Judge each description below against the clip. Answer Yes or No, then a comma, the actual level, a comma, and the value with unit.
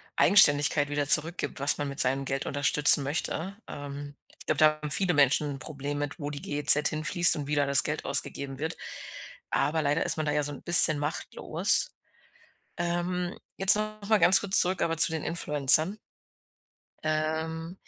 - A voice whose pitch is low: No, medium, 150 Hz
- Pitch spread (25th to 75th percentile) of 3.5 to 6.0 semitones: No, average, 2.7 semitones